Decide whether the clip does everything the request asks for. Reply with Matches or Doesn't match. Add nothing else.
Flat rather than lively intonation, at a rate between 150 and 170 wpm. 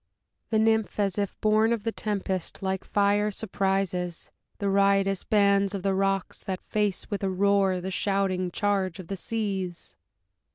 Matches